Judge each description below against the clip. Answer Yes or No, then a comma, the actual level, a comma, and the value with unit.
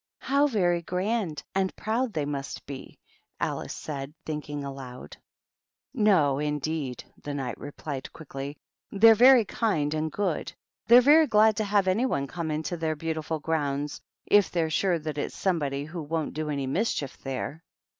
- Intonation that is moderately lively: No, wide, 5.7 semitones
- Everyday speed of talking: Yes, average, 165 wpm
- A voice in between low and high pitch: Yes, medium, 160 Hz